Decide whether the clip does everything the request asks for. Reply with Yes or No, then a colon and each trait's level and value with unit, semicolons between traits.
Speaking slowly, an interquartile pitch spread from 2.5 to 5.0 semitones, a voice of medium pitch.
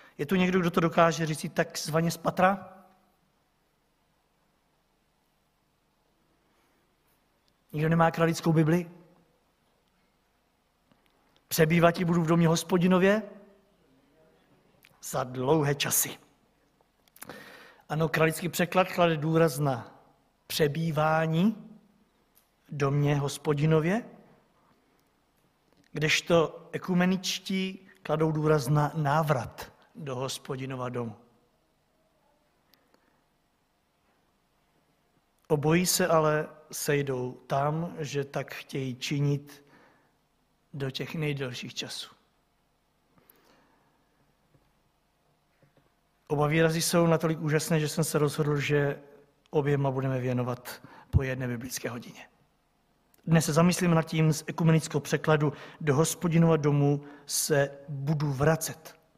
Yes: slow, 90 wpm; average, 2.9 semitones; medium, 160 Hz